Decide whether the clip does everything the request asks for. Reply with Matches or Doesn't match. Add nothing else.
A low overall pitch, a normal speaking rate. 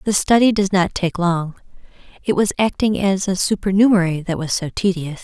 Doesn't match